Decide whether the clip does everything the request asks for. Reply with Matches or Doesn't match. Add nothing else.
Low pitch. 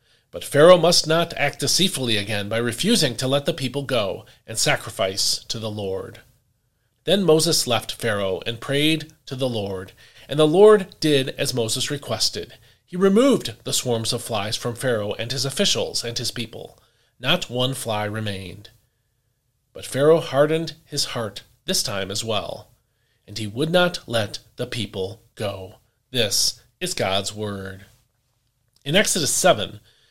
Matches